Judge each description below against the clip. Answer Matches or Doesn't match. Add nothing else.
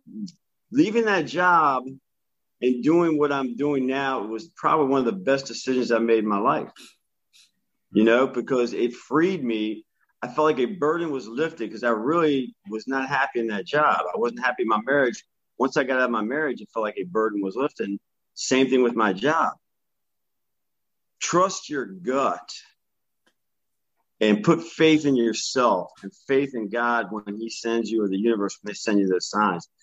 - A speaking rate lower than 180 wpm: Doesn't match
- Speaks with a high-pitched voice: Doesn't match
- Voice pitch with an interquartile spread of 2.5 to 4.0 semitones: Doesn't match